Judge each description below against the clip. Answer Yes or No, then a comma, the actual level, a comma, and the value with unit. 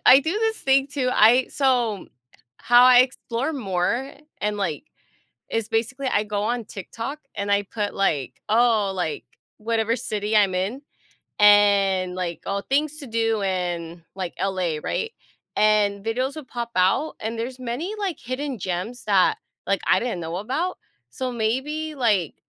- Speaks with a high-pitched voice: Yes, high, 225 Hz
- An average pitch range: Yes, average, 4.7 semitones